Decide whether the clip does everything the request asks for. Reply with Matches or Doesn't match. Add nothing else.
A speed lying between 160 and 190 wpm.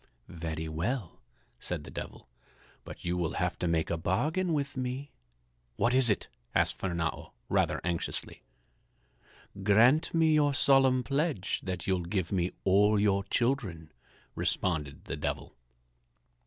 Doesn't match